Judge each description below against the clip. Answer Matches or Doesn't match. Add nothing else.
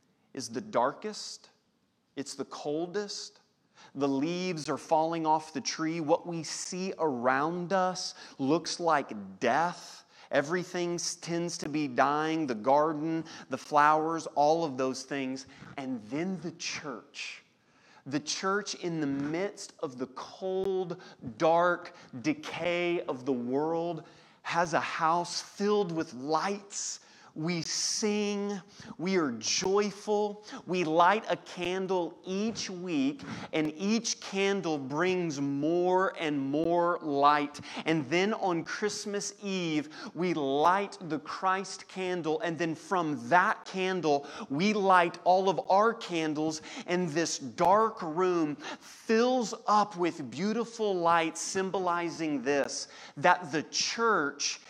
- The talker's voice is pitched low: Doesn't match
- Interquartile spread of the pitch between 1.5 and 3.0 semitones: Doesn't match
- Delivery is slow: Matches